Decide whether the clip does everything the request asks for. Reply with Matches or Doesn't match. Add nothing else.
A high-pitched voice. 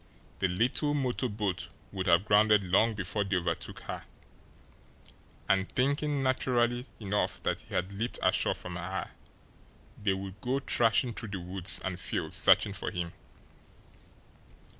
Doesn't match